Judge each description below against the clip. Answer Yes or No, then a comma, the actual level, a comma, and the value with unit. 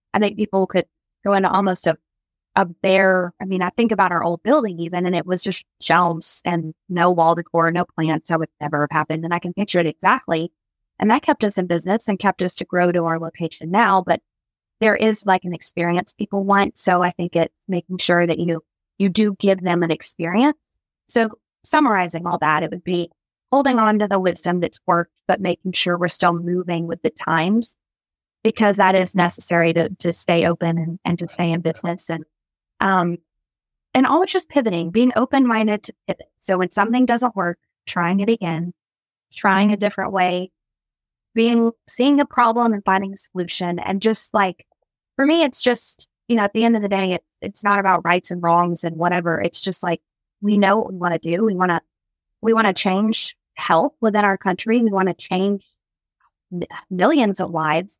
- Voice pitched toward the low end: No, medium, 185 Hz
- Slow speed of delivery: No, fast, 205 wpm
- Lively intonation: No, average, 3.4 semitones